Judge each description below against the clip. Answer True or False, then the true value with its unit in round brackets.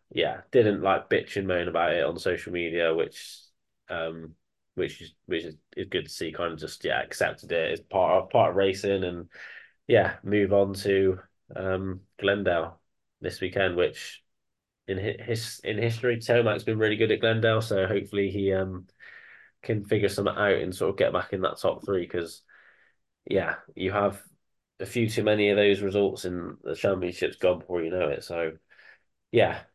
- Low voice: True (100 Hz)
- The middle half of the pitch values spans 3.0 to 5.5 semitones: False (2.4 semitones)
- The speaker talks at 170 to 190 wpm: True (180 wpm)